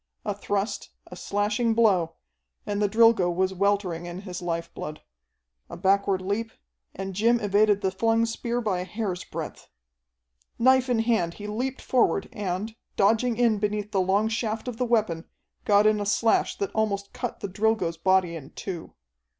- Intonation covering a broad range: No, average, 3.1 semitones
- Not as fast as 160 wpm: No, average, 170 wpm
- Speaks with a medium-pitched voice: No, high, 205 Hz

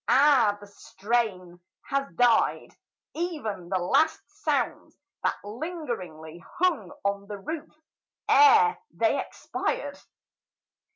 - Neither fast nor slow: No, slow, 100 wpm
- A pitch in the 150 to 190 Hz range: No, high, 225 Hz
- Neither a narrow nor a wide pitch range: No, wide, 8.1 semitones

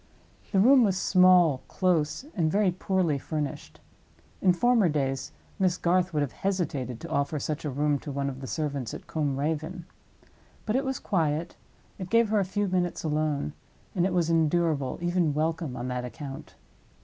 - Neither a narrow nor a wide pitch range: Yes, average, 4.2 semitones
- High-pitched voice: No, medium, 160 Hz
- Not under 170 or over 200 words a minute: Yes, average, 175 wpm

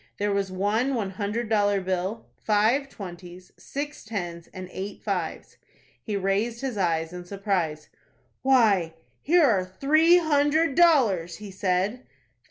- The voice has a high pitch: Yes, high, 205 Hz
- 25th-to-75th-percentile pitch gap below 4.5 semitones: No, wide, 5.5 semitones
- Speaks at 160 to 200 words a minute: No, slow, 135 wpm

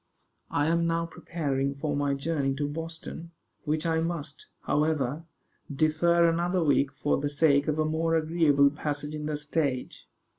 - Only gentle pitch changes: Yes, narrow, 2.3 semitones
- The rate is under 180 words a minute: Yes, average, 155 wpm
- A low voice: No, medium, 155 Hz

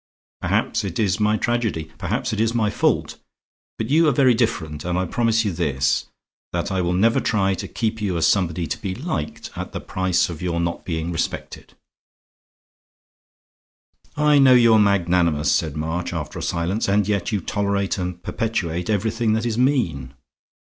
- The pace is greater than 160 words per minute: Yes, average, 175 wpm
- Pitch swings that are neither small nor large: Yes, average, 4.8 semitones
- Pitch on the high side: No, very low, 95 Hz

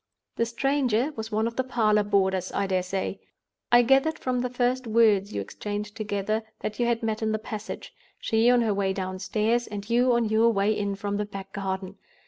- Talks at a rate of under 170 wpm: No, average, 200 wpm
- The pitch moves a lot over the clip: No, average, 3.0 semitones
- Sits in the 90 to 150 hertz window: No, high, 215 Hz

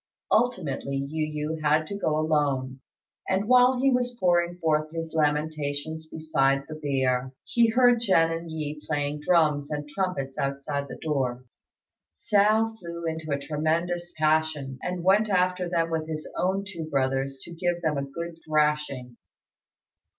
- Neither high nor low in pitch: Yes, medium, 155 Hz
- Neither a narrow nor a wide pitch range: Yes, average, 3.4 semitones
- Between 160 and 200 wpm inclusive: No, average, 150 wpm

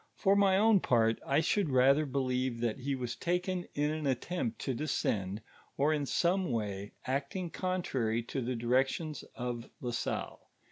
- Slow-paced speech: No, average, 160 wpm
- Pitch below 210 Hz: Yes, low, 135 Hz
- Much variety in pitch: Yes, wide, 6.0 semitones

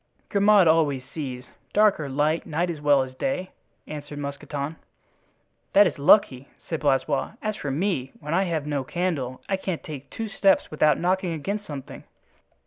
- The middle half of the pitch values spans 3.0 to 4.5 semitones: No, average, 4.9 semitones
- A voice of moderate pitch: Yes, medium, 155 Hz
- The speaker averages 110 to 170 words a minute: Yes, average, 165 wpm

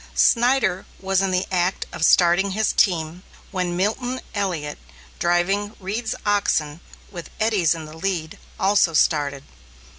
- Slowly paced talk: Yes, slow, 130 wpm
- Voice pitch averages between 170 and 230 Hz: Yes, medium, 185 Hz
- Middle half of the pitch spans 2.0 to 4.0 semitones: Yes, average, 3.5 semitones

